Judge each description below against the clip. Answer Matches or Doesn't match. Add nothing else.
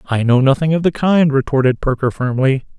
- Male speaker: Matches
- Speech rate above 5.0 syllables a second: Matches